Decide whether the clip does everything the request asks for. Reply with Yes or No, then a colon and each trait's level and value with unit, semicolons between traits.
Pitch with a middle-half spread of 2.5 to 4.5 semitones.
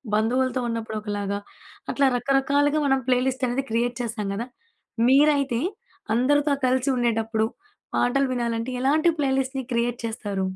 Yes: average, 2.9 semitones